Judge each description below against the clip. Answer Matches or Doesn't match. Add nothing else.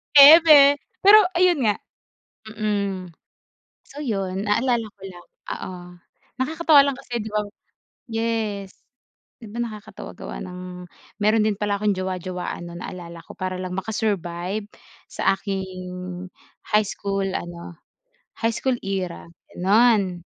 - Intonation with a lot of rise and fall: Doesn't match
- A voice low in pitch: Doesn't match